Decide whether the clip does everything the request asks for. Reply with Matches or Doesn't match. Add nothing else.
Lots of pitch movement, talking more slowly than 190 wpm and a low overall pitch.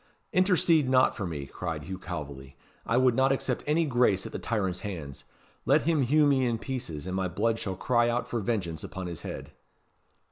Doesn't match